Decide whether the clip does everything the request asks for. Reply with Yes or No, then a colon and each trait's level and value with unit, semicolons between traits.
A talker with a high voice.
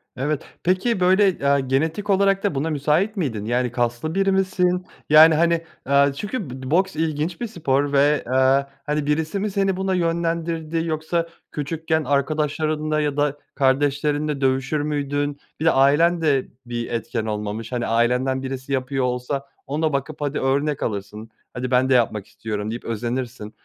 No: medium, 145 Hz